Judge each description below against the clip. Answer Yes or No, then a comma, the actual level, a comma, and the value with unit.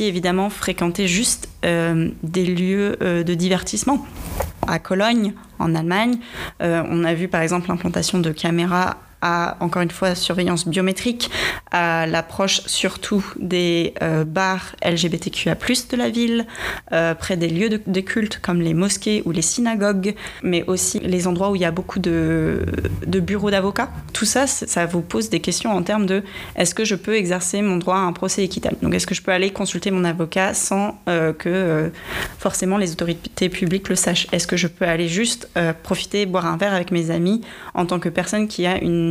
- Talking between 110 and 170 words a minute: No, average, 195 wpm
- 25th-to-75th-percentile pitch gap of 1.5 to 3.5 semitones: Yes, average, 2.9 semitones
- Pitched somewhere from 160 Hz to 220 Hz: Yes, medium, 185 Hz